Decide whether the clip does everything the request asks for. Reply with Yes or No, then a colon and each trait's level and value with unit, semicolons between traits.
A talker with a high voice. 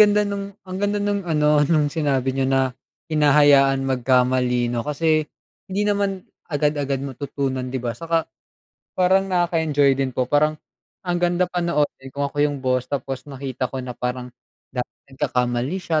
No: medium, 145 Hz